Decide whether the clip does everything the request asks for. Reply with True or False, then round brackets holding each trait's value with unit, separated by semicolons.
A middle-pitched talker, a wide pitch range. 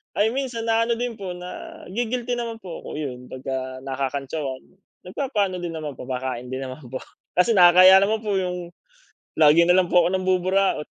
True (180 Hz; 8.0 semitones)